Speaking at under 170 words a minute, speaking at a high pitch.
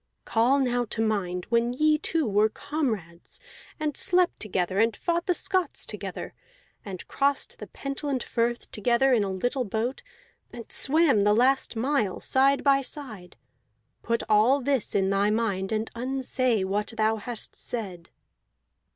Yes: average, 150 wpm; high, 235 Hz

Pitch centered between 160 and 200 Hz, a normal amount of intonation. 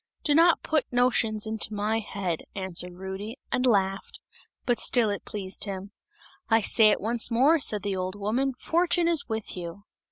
No: high, 215 Hz; average, 4.2 semitones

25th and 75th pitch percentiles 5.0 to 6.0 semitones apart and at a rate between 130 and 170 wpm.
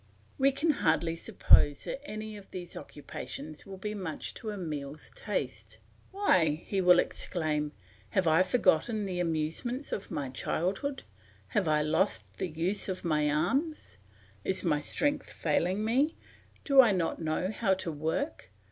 Yes: wide, 5.6 semitones; average, 150 wpm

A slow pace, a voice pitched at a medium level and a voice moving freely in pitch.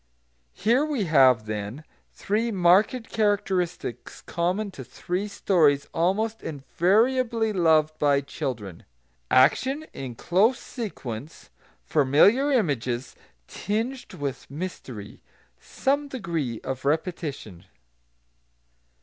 Yes: slow, 90 wpm; medium, 170 Hz; wide, 8.1 semitones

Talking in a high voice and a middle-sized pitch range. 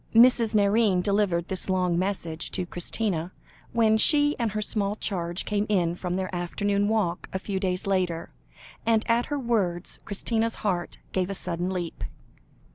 Yes: high, 195 Hz; average, 3.4 semitones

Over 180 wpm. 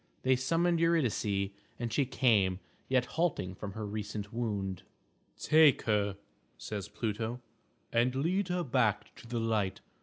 No: average, 140 wpm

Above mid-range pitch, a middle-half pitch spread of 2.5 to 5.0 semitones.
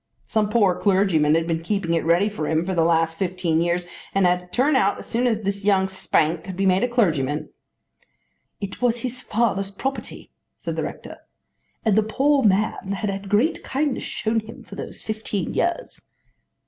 Yes: high, 195 Hz; average, 4.2 semitones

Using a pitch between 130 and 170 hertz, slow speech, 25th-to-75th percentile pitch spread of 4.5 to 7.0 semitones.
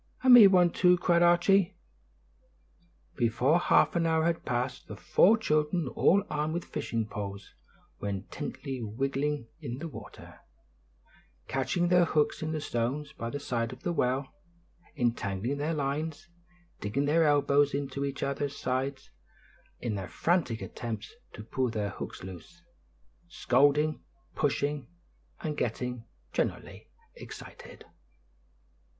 Yes: medium, 140 Hz; slow, 130 wpm; average, 4.8 semitones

